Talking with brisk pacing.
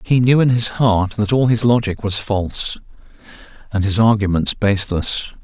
No: average, 165 wpm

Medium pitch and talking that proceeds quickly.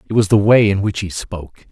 No: low, 100 Hz; fast, 280 wpm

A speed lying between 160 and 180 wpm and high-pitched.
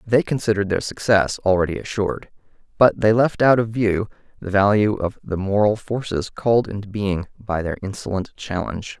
No: average, 165 wpm; low, 105 Hz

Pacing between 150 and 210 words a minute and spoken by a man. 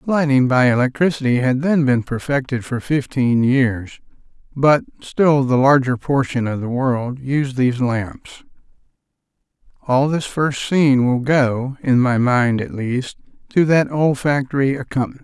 No: average, 140 wpm; male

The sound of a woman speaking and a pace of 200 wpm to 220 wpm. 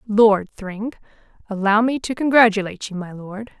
No: female; slow, 135 wpm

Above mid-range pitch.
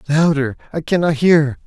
No: medium, 150 Hz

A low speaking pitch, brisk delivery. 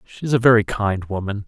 Yes: low, 105 Hz; fast, 245 wpm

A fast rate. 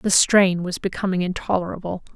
No: average, 140 wpm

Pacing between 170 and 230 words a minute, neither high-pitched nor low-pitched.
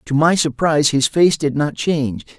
Yes: average, 200 wpm; medium, 150 Hz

